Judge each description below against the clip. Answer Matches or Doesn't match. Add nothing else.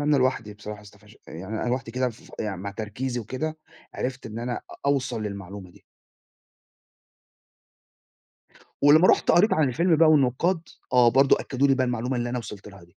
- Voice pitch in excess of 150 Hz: Doesn't match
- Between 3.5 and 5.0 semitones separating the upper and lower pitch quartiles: Matches